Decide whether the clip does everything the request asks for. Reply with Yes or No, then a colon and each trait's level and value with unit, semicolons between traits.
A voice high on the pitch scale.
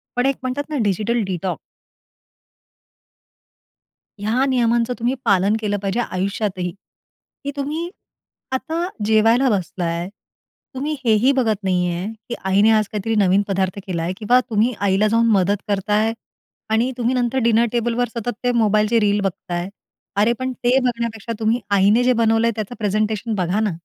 Yes: high, 220 Hz